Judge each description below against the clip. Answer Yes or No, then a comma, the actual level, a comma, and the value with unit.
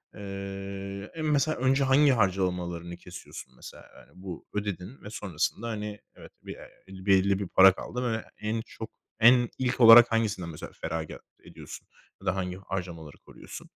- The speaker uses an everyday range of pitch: Yes, average, 3.8 semitones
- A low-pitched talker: Yes, low, 100 Hz